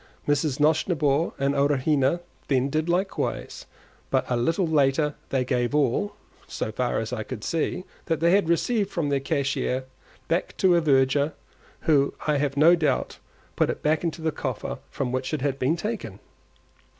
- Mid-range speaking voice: Yes, medium, 145 Hz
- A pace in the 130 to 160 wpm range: No, average, 170 wpm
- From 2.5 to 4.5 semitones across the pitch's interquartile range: Yes, average, 3.5 semitones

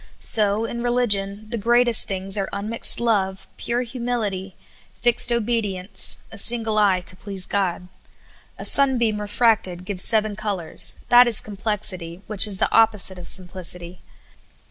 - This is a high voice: Yes, high, 210 Hz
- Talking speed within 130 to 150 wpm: Yes, average, 140 wpm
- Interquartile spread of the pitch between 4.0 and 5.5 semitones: No, average, 3.5 semitones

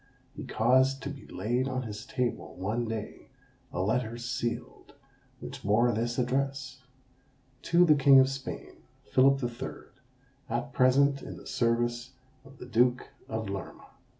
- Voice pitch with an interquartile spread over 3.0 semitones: No, narrow, 2.4 semitones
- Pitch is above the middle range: No, low, 125 Hz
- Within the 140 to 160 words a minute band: Yes, average, 150 wpm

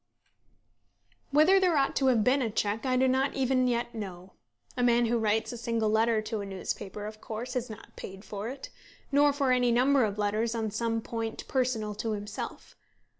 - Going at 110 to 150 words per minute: No, average, 195 wpm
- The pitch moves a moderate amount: Yes, average, 3.0 semitones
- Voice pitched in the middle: No, high, 230 Hz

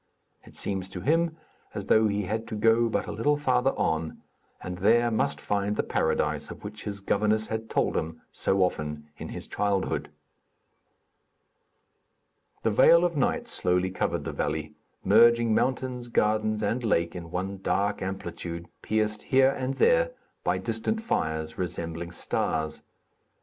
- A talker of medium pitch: No, low, 105 Hz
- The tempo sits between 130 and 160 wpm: Yes, average, 150 wpm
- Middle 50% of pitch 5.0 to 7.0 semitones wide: No, average, 4.6 semitones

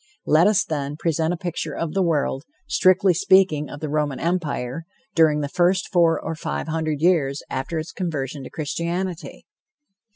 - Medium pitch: Yes, medium, 160 Hz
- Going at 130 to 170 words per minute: Yes, average, 165 wpm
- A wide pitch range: No, average, 3.0 semitones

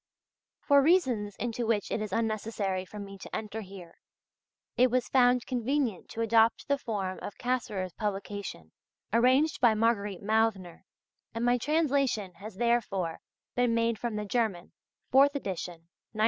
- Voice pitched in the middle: No, high, 225 Hz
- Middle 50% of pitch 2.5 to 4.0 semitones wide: Yes, average, 3.6 semitones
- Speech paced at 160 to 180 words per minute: No, average, 150 wpm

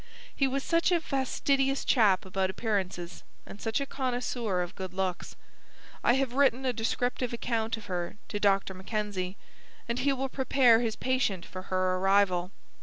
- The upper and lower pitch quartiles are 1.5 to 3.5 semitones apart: No, wide, 5.4 semitones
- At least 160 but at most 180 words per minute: Yes, average, 165 wpm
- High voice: Yes, high, 225 Hz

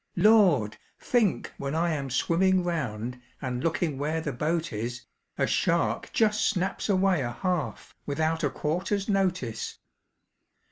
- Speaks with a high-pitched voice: No, medium, 160 Hz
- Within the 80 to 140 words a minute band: Yes, slow, 135 wpm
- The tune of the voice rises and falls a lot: Yes, wide, 5.7 semitones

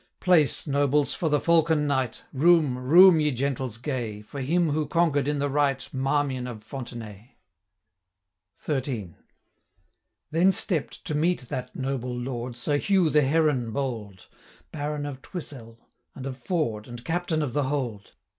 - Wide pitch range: No, average, 3.5 semitones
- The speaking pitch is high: No, medium, 140 Hz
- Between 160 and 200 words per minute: No, average, 150 wpm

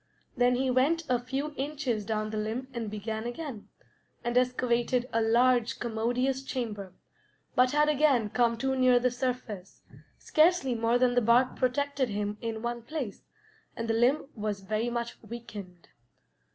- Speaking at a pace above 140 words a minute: Yes, average, 155 wpm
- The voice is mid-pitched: No, high, 240 Hz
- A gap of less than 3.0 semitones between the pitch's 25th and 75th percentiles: Yes, narrow, 2.6 semitones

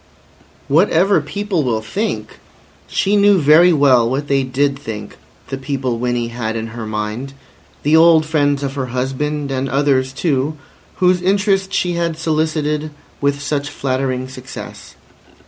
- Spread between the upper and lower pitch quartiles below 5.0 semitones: Yes, average, 3.7 semitones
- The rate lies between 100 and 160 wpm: Yes, average, 140 wpm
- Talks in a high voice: No, medium, 140 Hz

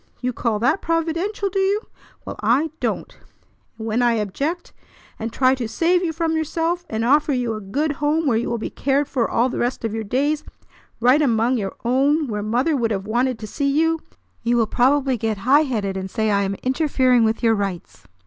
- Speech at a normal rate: No, fast, 210 wpm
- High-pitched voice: Yes, very high, 255 Hz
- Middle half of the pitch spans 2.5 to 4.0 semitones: No, average, 5.2 semitones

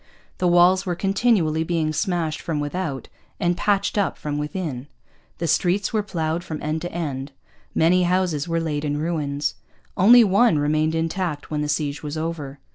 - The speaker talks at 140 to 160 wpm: No, average, 170 wpm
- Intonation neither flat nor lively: Yes, average, 3.4 semitones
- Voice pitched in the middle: Yes, medium, 165 Hz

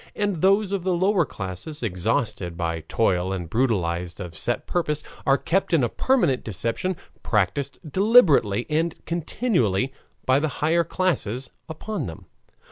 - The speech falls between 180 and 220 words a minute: No, average, 140 wpm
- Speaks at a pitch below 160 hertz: Yes, low, 135 Hz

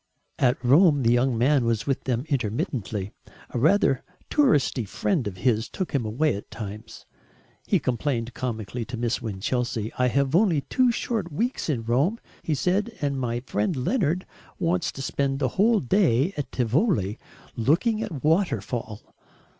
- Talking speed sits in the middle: Yes, average, 160 wpm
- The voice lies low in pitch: Yes, low, 130 Hz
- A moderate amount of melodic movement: No, wide, 6.3 semitones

